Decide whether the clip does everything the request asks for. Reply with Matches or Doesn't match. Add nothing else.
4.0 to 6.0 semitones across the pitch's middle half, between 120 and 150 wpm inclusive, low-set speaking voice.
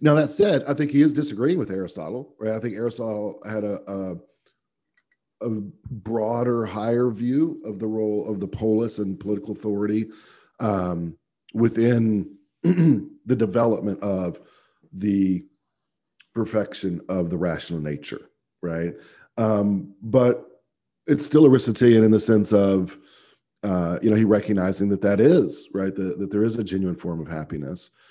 Doesn't match